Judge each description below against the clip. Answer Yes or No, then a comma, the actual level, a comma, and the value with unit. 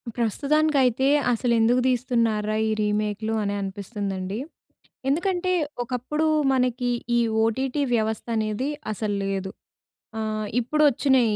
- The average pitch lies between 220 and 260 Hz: Yes, high, 235 Hz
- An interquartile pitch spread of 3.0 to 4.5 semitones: Yes, average, 3.7 semitones